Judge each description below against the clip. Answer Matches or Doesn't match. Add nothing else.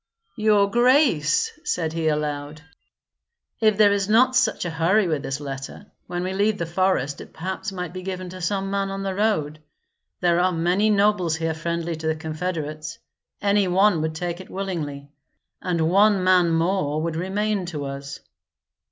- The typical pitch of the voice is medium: Matches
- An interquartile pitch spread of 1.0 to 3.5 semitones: Doesn't match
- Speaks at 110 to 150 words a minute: Doesn't match